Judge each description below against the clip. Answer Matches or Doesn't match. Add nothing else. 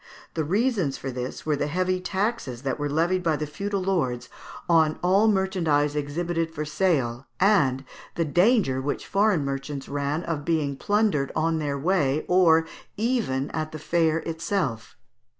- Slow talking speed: Doesn't match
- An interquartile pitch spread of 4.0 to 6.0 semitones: Matches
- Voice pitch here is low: Doesn't match